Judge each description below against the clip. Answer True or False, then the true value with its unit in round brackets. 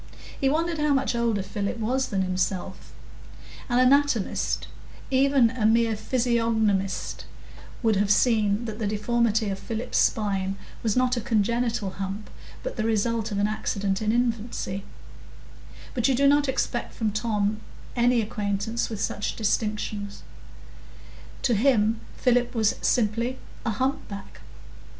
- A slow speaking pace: True (130 wpm)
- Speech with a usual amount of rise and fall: True (3.0 semitones)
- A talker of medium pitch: False (225 Hz)